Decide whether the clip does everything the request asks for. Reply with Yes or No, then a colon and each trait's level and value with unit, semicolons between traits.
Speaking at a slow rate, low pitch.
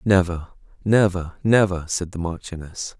Yes: slow, 120 wpm; very low, 90 Hz